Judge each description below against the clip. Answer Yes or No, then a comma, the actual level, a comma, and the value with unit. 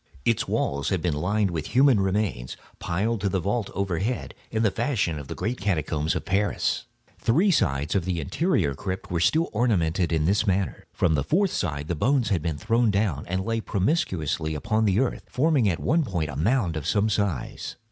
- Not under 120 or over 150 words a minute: No, average, 195 wpm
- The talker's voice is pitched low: Yes, very low, 95 Hz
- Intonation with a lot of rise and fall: Yes, wide, 5.7 semitones